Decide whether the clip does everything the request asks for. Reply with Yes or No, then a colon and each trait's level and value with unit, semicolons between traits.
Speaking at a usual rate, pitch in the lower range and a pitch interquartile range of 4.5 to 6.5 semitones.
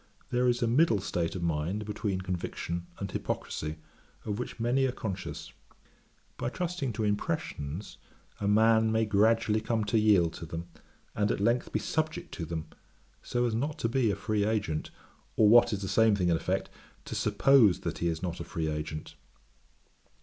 Yes: average, 180 wpm; low, 105 Hz; average, 5.0 semitones